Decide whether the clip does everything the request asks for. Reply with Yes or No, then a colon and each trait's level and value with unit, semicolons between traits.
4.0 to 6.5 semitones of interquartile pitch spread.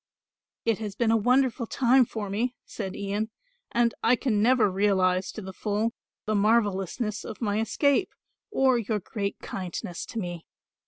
No: average, 3.0 semitones